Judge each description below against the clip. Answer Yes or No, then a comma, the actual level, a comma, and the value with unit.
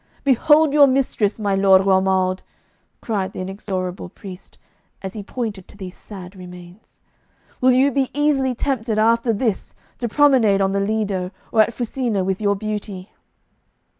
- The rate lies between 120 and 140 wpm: No, average, 150 wpm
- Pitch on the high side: Yes, high, 210 Hz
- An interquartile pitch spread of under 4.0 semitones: No, average, 4.4 semitones